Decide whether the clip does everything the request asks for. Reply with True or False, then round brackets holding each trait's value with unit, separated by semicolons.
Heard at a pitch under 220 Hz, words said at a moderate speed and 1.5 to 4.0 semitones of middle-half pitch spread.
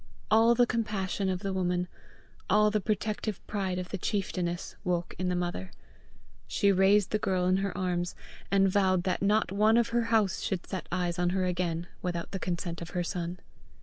True (185 Hz; 190 wpm; 2.5 semitones)